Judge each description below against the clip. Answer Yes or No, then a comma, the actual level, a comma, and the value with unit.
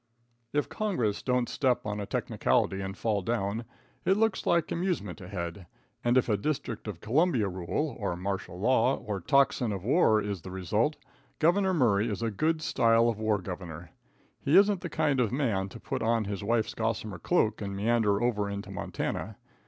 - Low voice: Yes, low, 110 Hz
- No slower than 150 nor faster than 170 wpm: No, average, 185 wpm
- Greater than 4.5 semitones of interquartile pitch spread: Yes, average, 5.2 semitones